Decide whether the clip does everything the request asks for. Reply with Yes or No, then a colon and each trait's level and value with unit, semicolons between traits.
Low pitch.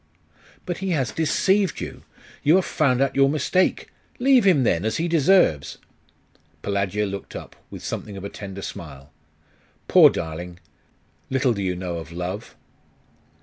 Yes: low, 110 Hz